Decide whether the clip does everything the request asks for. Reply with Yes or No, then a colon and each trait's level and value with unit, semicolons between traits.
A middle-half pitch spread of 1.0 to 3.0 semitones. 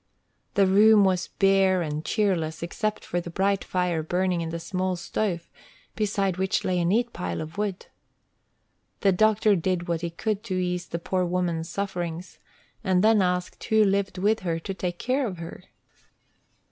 Yes: narrow, 2.5 semitones